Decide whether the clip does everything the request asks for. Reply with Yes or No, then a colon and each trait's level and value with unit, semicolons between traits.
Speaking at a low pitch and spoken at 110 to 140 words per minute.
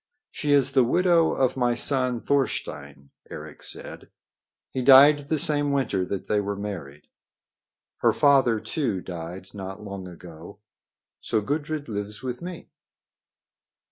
Yes: low, 120 Hz; slow, 135 wpm